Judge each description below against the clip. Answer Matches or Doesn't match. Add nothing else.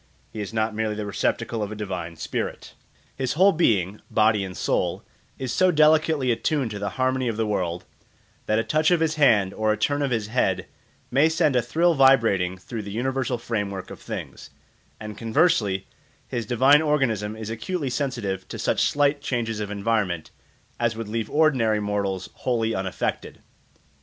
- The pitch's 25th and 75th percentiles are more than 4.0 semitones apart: Matches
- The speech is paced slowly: Doesn't match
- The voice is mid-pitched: Doesn't match